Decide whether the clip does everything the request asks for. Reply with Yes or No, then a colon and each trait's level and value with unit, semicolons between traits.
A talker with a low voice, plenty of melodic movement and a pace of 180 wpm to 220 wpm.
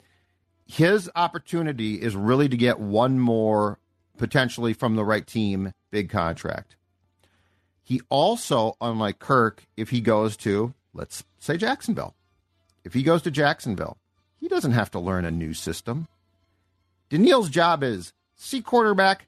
No: low, 110 Hz; wide, 6.0 semitones; slow, 135 wpm